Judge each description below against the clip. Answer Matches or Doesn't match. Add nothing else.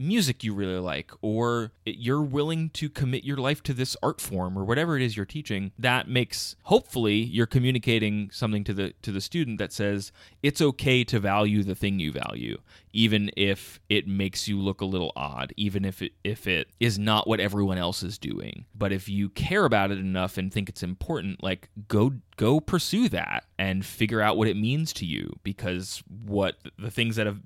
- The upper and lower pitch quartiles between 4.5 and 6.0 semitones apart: Doesn't match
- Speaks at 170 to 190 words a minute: Doesn't match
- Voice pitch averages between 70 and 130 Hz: Matches